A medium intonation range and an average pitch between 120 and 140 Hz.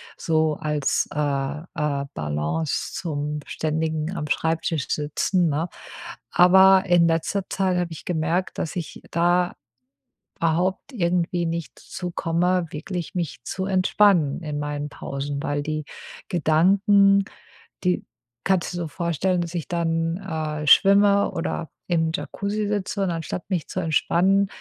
No: average, 3.2 semitones; medium, 170 Hz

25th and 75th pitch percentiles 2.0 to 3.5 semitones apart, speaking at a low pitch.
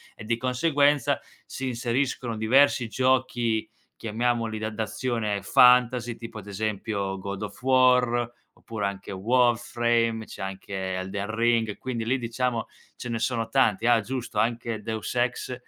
Yes: narrow, 2.4 semitones; low, 115 Hz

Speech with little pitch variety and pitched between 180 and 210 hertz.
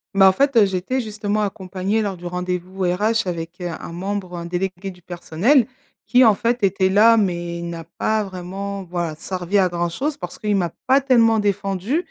No: average, 3.2 semitones; high, 190 Hz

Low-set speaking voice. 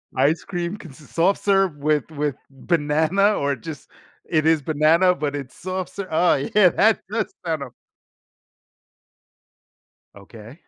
No: medium, 155 Hz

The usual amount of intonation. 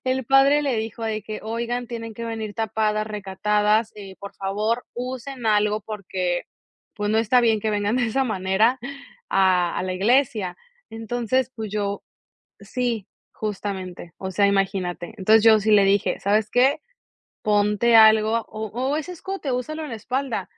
Yes: average, 3.0 semitones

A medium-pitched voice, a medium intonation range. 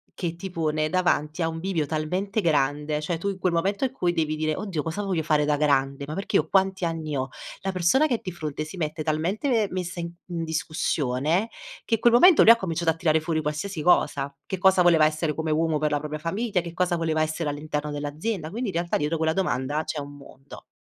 Yes: medium, 160 Hz; average, 3.3 semitones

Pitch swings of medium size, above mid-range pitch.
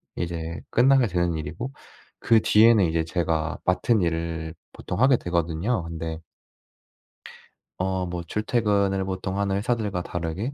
No: average, 4.3 semitones; very low, 90 Hz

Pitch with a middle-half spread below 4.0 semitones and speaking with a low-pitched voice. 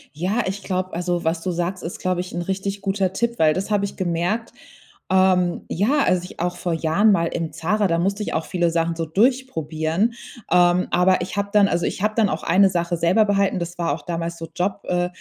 No: average, 2.7 semitones; medium, 180 Hz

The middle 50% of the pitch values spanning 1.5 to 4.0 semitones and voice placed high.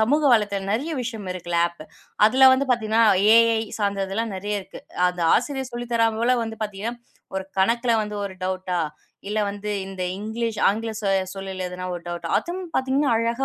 Yes: average, 3.5 semitones; high, 220 Hz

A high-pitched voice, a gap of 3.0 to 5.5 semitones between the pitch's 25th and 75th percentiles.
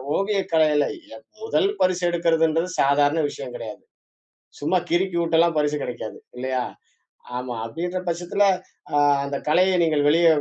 No: medium, 165 Hz; average, 3.3 semitones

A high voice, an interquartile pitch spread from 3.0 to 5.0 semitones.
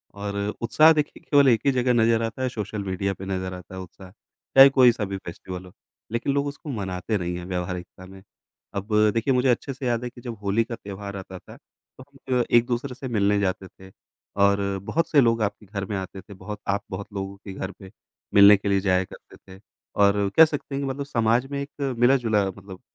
No: low, 105 Hz; average, 4.5 semitones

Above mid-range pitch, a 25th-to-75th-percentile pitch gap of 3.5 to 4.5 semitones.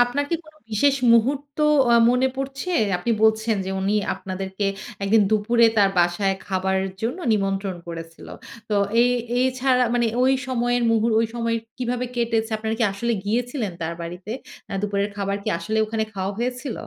Yes: high, 220 Hz; average, 3.9 semitones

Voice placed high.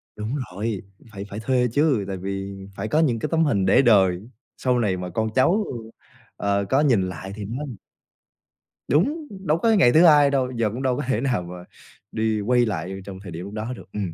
No: low, 110 Hz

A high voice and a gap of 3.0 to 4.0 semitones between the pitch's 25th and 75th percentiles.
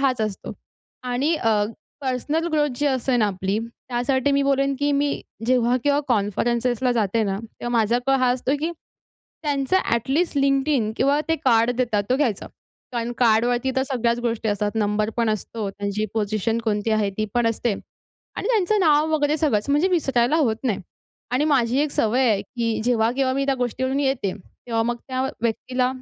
Yes: high, 245 Hz; average, 3.6 semitones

